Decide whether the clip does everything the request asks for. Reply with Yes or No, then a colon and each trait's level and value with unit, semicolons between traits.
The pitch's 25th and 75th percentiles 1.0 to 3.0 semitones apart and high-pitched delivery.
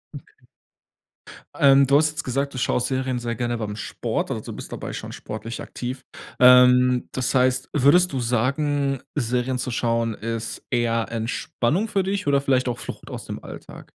No: average, 2.7 semitones; low, 125 Hz